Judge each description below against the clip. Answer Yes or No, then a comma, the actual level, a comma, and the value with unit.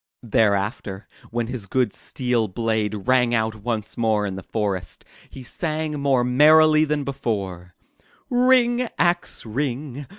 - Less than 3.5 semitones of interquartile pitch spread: No, wide, 5.6 semitones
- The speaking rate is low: Yes, slow, 130 wpm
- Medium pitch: No, low, 120 Hz